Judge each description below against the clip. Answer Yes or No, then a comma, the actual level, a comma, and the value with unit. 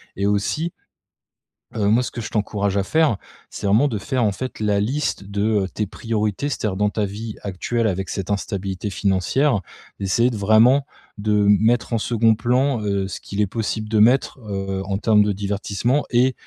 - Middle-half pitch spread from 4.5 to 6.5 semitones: No, average, 3.0 semitones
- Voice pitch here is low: Yes, low, 105 Hz